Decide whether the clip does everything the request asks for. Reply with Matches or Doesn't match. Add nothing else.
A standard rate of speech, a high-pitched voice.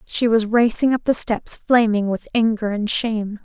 Matches